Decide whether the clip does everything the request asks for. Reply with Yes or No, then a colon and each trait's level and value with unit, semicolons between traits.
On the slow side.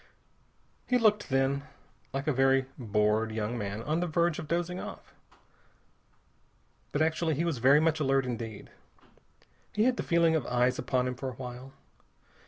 No: average, 165 wpm